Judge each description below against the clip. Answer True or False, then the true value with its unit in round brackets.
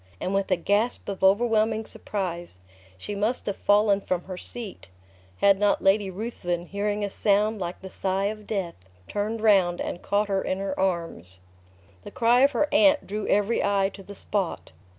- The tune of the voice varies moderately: False (2.0 semitones)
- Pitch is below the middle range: False (200 Hz)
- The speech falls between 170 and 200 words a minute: True (180 wpm)